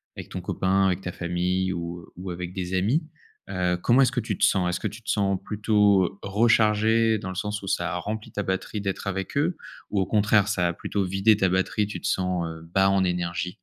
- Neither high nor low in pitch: No, very low, 95 Hz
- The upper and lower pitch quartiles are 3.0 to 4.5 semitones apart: No, narrow, 2.6 semitones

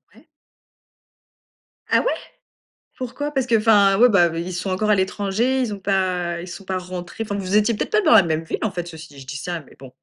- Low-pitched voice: No, high, 190 Hz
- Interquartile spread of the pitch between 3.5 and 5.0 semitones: Yes, average, 3.9 semitones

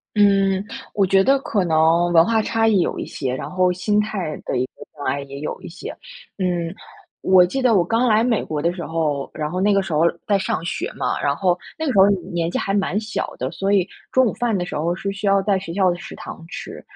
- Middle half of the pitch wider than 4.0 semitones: No, average, 3.5 semitones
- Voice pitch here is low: No, high, 190 Hz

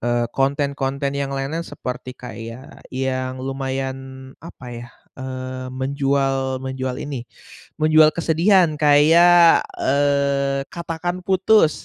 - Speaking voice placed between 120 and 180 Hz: Yes, low, 135 Hz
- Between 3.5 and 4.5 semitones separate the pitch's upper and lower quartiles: No, average, 2.7 semitones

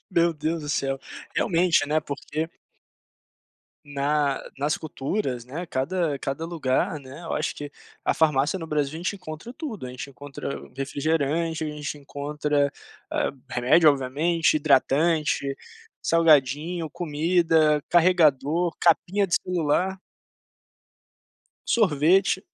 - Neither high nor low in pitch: Yes, medium, 155 Hz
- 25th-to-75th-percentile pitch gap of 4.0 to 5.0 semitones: No, average, 3.0 semitones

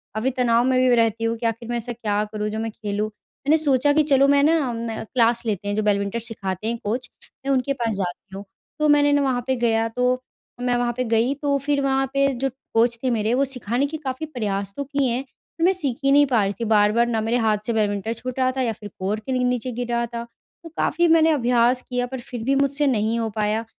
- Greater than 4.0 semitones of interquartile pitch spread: No, average, 3.4 semitones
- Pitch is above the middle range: Yes, high, 240 Hz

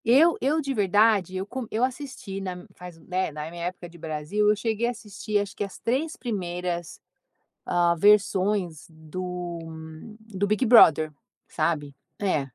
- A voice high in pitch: Yes, high, 195 Hz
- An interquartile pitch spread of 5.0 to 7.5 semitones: No, average, 4.1 semitones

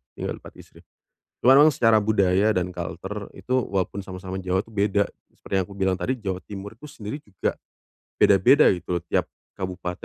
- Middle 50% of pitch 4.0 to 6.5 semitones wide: No, average, 2.9 semitones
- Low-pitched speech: Yes, low, 100 Hz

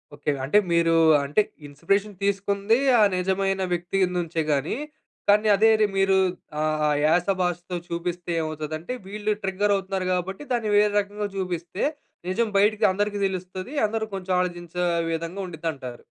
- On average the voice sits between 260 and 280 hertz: No, high, 190 Hz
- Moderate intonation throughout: Yes, average, 3.2 semitones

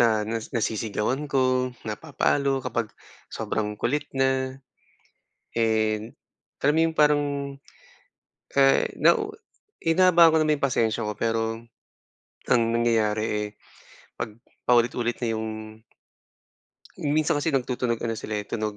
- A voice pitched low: Yes, low, 120 Hz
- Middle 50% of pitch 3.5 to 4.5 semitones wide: Yes, average, 4.1 semitones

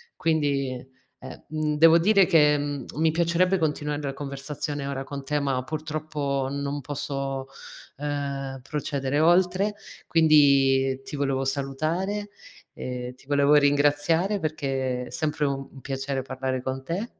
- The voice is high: No, medium, 145 Hz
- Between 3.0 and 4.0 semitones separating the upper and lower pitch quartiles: No, narrow, 2.5 semitones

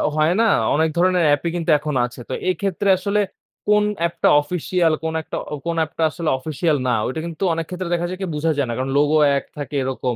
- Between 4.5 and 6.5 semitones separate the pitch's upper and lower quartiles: No, average, 3.3 semitones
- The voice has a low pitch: No, medium, 160 Hz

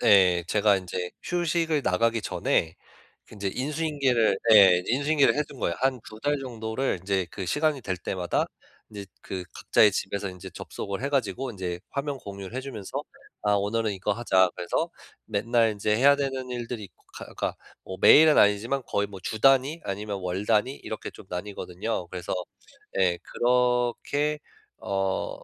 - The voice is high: No, low, 110 Hz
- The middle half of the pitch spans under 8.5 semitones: Yes, wide, 5.5 semitones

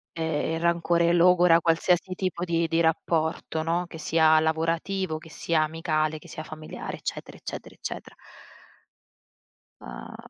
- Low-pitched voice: No, medium, 165 Hz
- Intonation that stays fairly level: Yes, narrow, 1.3 semitones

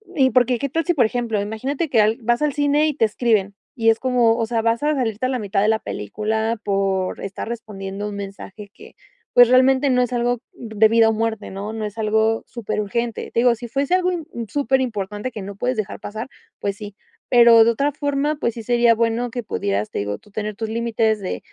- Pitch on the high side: Yes, high, 230 Hz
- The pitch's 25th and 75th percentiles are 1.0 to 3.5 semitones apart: Yes, average, 2.9 semitones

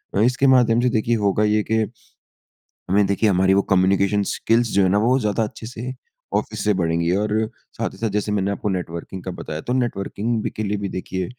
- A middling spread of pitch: Yes, average, 3.0 semitones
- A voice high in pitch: No, low, 105 Hz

